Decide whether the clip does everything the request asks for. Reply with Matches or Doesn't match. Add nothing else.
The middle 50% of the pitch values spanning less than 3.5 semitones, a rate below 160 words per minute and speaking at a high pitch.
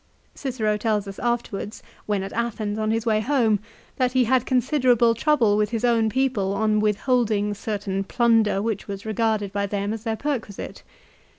Doesn't match